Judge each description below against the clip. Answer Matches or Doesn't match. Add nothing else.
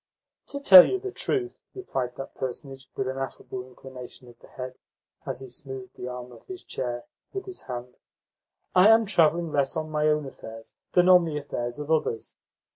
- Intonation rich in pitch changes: Matches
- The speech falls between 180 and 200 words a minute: Matches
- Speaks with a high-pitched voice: Doesn't match